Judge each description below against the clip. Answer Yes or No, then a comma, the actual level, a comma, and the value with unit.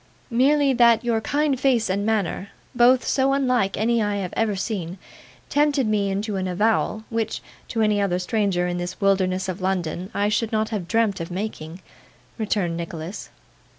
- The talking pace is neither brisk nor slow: Yes, average, 170 wpm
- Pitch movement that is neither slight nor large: Yes, average, 3.7 semitones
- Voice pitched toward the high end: Yes, high, 210 Hz